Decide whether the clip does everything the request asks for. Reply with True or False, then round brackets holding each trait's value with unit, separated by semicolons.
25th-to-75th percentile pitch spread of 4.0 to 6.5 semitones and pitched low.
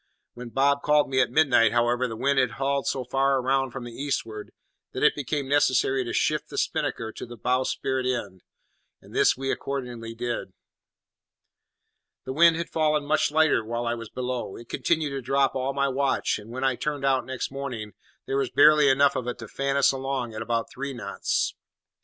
False (2.6 semitones; 130 Hz)